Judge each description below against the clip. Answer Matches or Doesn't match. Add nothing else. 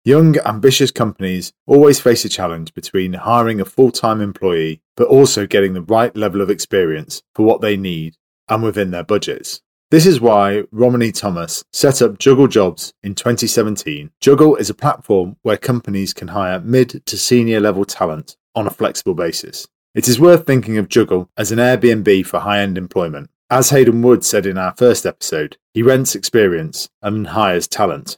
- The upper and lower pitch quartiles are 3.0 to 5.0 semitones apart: Matches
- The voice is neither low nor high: Doesn't match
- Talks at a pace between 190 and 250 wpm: Doesn't match